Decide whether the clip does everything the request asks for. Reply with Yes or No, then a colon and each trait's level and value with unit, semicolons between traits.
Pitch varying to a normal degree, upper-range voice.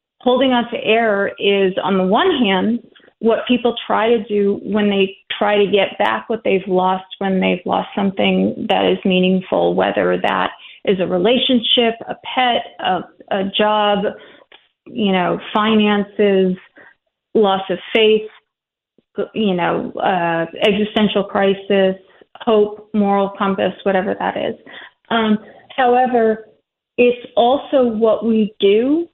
Yes: average, 3.0 semitones; high, 210 Hz